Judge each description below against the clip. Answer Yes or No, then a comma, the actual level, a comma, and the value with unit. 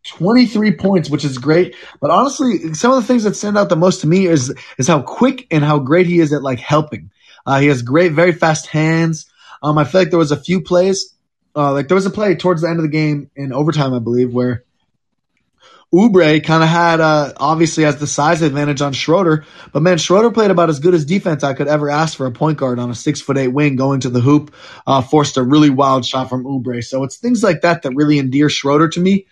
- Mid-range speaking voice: Yes, medium, 155 Hz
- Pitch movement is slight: No, average, 4.1 semitones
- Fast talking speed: Yes, fast, 250 wpm